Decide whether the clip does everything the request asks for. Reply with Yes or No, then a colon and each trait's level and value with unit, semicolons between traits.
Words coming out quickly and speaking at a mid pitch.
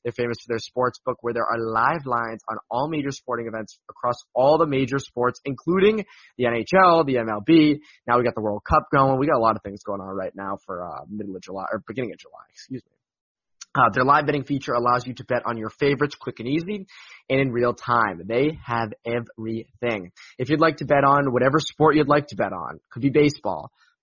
No: fast, 230 wpm; low, 125 Hz